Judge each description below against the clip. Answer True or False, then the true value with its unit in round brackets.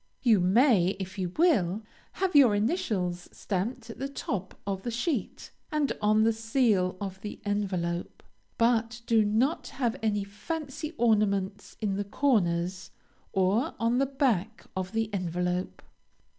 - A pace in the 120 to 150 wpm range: True (145 wpm)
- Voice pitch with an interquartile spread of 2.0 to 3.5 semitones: False (4.1 semitones)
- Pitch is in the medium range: False (210 Hz)